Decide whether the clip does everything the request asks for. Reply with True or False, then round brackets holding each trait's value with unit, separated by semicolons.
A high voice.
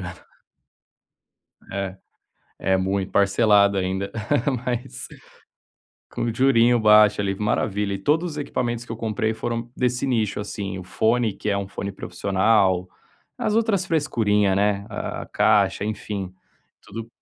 False (105 Hz)